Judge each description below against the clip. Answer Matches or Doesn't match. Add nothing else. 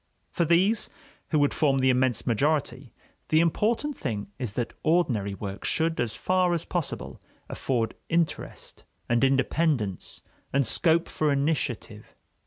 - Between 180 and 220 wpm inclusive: Doesn't match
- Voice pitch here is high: Doesn't match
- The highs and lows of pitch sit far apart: Matches